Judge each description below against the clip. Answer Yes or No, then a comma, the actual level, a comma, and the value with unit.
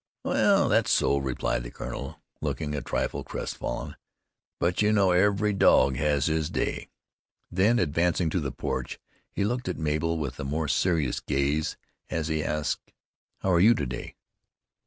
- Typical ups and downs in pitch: Yes, average, 4.5 semitones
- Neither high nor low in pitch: No, very low, 80 Hz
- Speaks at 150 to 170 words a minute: Yes, average, 165 wpm